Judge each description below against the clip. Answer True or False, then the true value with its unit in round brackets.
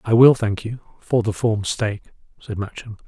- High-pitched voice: False (110 Hz)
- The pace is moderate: True (195 wpm)